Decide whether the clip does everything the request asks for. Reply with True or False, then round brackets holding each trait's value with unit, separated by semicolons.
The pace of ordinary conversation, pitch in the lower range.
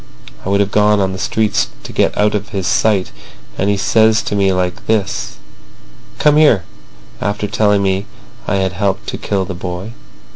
True (185 wpm; 100 Hz)